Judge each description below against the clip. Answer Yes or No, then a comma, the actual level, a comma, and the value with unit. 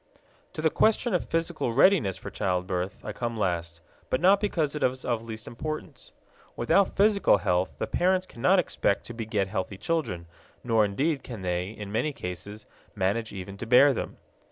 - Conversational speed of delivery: Yes, average, 175 wpm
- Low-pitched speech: Yes, low, 115 Hz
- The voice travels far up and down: Yes, wide, 8.2 semitones